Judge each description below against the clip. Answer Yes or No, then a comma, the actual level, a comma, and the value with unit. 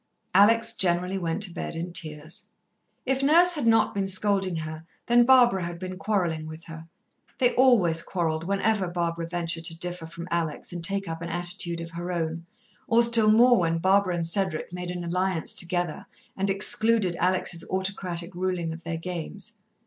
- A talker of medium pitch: Yes, medium, 180 Hz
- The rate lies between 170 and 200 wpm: Yes, average, 175 wpm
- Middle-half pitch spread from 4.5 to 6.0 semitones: No, average, 2.9 semitones